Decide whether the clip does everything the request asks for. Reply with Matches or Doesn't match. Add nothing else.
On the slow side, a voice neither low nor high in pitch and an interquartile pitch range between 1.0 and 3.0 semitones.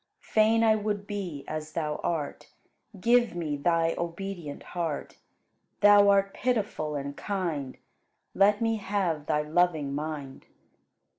Doesn't match